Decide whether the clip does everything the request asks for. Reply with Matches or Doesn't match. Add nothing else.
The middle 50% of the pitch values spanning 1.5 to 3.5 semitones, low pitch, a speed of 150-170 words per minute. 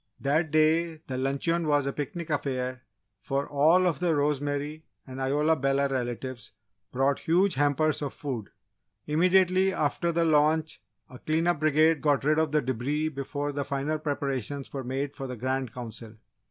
Doesn't match